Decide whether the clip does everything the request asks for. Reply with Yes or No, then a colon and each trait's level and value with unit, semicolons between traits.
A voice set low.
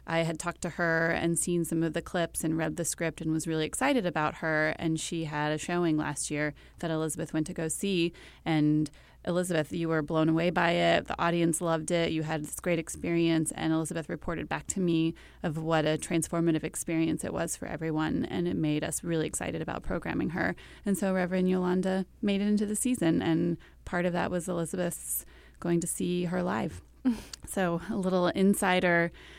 No: medium, 170 Hz